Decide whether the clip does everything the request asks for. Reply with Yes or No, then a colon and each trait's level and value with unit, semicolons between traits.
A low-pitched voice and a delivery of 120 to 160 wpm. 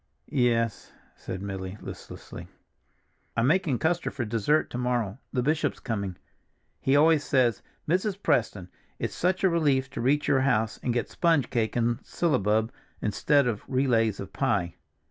Yes: low, 125 Hz; average, 150 wpm